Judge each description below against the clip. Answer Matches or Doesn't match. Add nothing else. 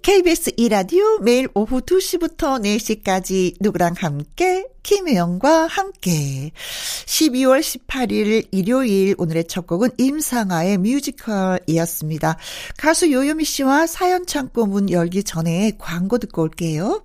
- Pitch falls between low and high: Doesn't match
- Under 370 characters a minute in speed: Matches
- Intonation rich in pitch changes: Matches